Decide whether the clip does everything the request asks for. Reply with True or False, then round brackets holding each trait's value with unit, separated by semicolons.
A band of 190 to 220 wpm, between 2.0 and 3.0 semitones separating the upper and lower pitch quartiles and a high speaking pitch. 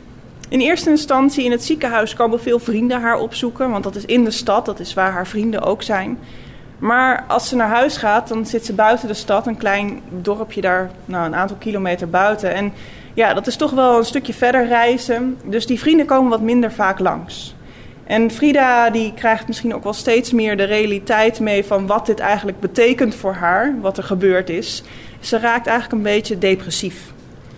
False (200 wpm; 3.4 semitones; 220 Hz)